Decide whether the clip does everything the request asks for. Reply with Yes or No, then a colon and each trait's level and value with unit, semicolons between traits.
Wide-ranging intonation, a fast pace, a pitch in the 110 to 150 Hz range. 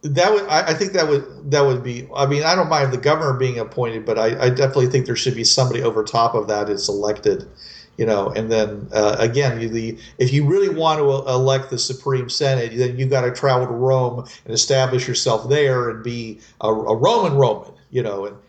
No: average, 3.3 semitones; fast, 225 wpm; low, 125 Hz